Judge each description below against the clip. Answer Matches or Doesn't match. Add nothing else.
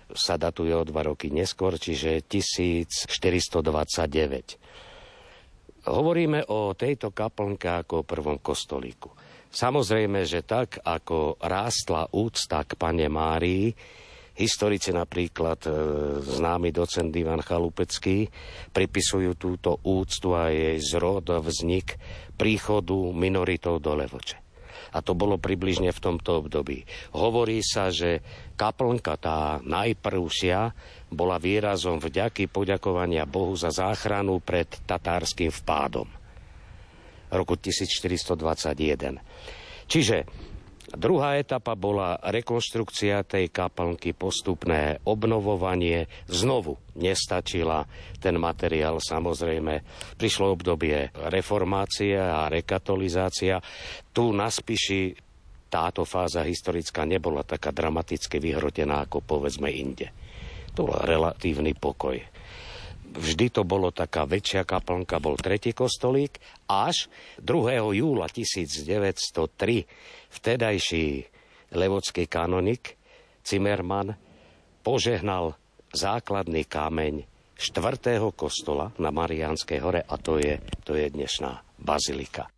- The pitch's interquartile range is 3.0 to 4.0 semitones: Matches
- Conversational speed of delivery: Doesn't match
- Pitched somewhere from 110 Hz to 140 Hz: Doesn't match